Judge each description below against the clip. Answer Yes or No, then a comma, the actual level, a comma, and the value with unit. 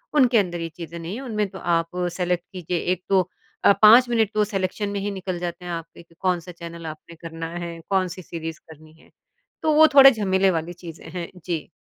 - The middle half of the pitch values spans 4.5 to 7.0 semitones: No, average, 3.2 semitones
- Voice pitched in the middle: Yes, medium, 180 Hz